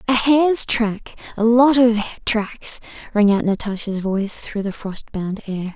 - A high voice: Yes, high, 220 Hz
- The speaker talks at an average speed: Yes, average, 165 wpm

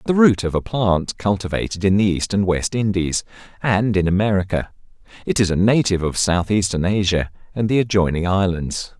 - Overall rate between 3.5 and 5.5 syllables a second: Yes, 5.3 syllables/s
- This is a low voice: Yes, low, 100 Hz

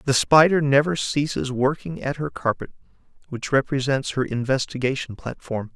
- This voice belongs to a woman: No, male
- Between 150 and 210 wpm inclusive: No, slow, 135 wpm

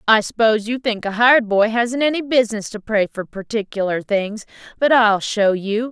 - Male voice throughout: No, female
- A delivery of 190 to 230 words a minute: Yes, average, 195 wpm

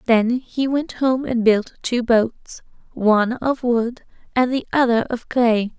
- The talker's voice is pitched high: Yes, high, 240 Hz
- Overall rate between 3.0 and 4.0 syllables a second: Yes, 3.7 syllables/s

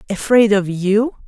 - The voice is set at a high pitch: Yes, high, 210 Hz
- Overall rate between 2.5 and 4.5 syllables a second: Yes, 4.2 syllables/s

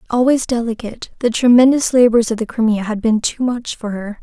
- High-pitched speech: Yes, high, 230 Hz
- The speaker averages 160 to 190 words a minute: No, average, 200 wpm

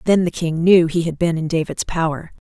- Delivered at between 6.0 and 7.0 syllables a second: No, 5.4 syllables/s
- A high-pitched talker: No, medium, 165 Hz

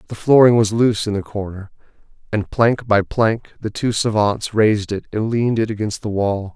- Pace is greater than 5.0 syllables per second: Yes, 5.2 syllables/s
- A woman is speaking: No, male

